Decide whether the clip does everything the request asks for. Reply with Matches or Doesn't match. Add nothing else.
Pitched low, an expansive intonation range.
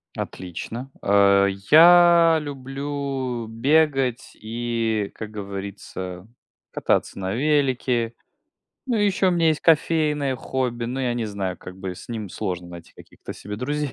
Matches